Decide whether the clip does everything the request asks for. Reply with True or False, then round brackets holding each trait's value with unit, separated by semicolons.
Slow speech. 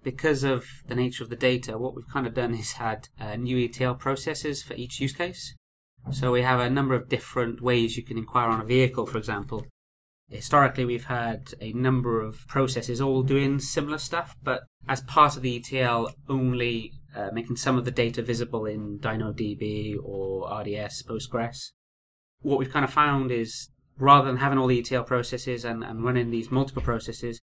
False (190 wpm)